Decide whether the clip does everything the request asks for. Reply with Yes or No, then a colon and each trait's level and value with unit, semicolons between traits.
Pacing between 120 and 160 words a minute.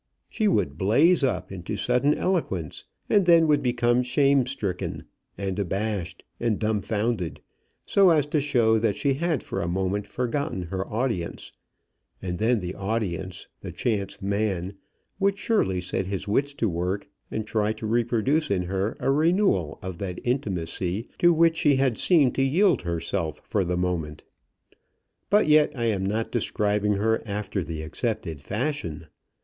Yes: average, 155 wpm